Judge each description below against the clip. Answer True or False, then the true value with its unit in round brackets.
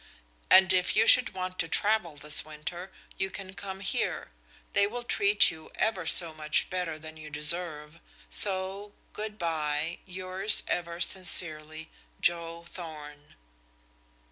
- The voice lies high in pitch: False (175 Hz)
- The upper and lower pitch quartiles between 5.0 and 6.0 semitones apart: False (3.5 semitones)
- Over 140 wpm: False (135 wpm)